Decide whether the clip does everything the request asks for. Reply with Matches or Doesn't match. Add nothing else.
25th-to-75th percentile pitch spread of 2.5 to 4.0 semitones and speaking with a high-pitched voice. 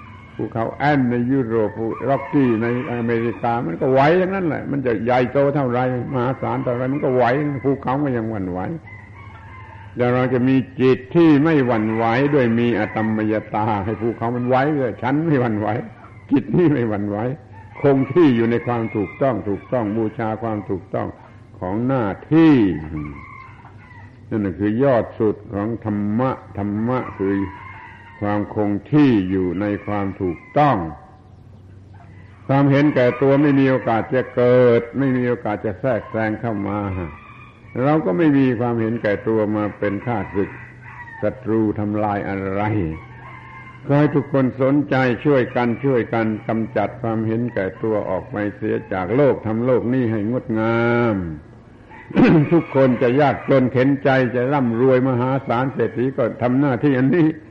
Doesn't match